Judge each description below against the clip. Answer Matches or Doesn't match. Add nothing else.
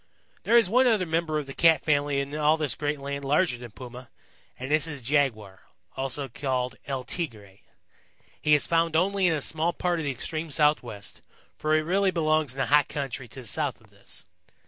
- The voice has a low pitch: Doesn't match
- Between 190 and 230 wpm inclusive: Matches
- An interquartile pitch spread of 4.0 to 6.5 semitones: Doesn't match